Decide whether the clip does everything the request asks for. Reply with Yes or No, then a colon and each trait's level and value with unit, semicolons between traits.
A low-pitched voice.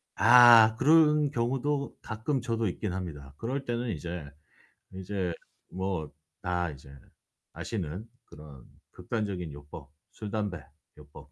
Yes: low, 100 Hz